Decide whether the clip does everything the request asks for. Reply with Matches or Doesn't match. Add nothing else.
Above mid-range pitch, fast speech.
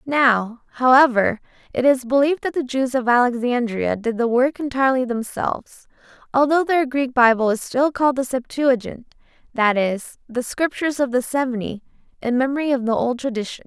Doesn't match